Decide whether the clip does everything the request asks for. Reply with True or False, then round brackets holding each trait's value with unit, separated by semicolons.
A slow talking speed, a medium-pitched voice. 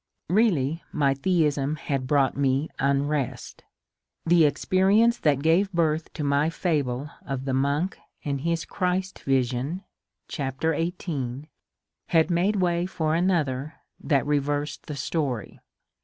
True (125 wpm; 150 Hz)